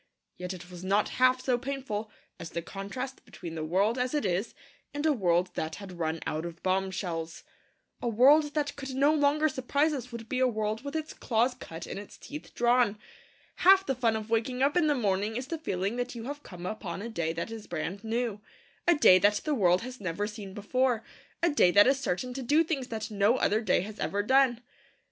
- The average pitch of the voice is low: No, high, 225 Hz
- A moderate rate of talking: No, fast, 220 wpm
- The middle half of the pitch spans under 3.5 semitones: No, wide, 5.5 semitones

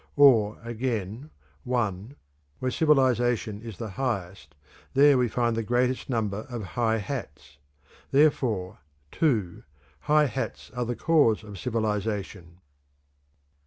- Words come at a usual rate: No, slow, 115 wpm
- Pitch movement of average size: Yes, average, 3.8 semitones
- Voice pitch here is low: Yes, low, 115 Hz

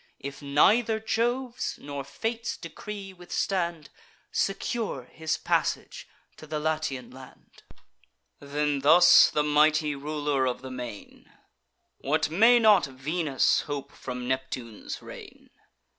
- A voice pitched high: No, medium, 150 Hz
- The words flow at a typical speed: No, slow, 115 wpm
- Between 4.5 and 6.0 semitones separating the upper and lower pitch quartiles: Yes, wide, 5.4 semitones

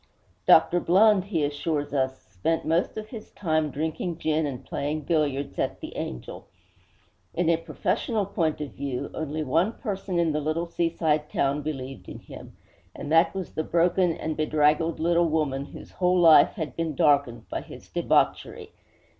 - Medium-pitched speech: Yes, medium, 160 Hz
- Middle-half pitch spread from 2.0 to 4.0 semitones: Yes, average, 2.8 semitones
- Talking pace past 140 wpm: Yes, average, 165 wpm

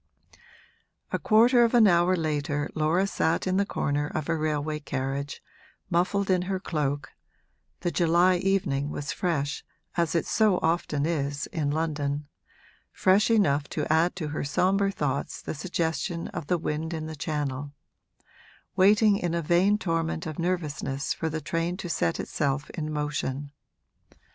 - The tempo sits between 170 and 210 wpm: No, average, 155 wpm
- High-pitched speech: No, medium, 160 Hz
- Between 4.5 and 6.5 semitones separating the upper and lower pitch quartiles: No, average, 3.7 semitones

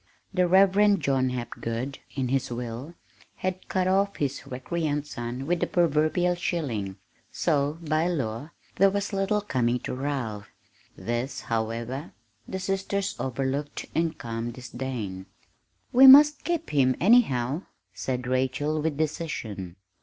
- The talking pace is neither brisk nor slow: No, slow, 130 wpm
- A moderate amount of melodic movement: No, wide, 6.5 semitones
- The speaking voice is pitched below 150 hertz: Yes, medium, 140 Hz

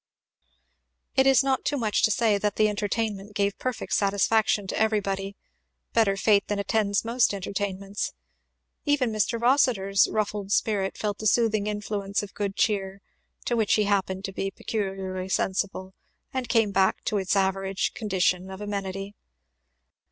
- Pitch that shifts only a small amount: Yes, narrow, 1.9 semitones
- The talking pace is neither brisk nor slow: Yes, average, 150 wpm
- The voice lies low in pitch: No, high, 205 Hz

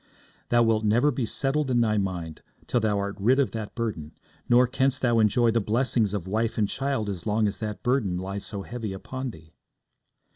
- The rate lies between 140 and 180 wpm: No, fast, 205 wpm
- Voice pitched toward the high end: No, low, 110 Hz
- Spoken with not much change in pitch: No, average, 3.5 semitones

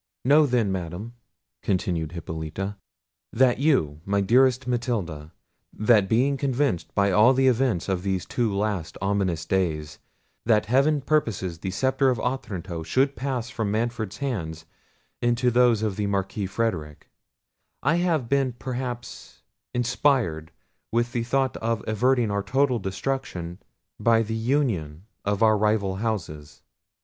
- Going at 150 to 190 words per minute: No, slow, 135 wpm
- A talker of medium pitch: No, low, 110 Hz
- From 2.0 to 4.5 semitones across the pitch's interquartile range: No, average, 5.1 semitones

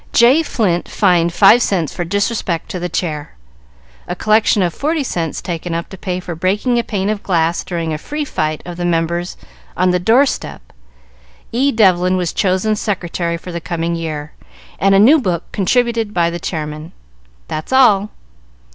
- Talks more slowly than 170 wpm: No, average, 175 wpm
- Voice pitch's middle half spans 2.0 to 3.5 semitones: No, average, 4.1 semitones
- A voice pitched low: No, medium, 180 Hz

